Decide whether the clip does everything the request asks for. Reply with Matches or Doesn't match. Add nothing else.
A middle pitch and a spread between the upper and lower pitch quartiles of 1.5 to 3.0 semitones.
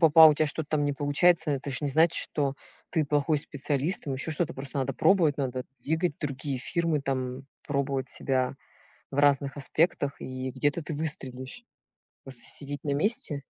Matches